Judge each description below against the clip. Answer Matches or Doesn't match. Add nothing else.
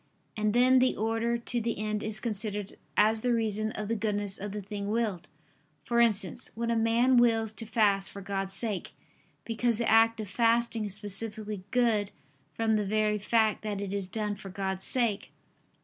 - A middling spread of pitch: Doesn't match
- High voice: Matches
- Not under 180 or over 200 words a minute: Matches